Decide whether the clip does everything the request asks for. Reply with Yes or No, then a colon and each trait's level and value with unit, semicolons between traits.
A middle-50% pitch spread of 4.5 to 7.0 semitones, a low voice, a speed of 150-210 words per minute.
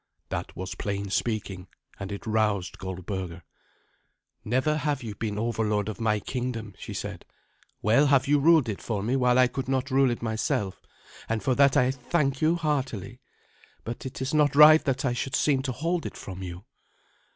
Yes: average, 4.8 semitones; low, 120 Hz; average, 185 wpm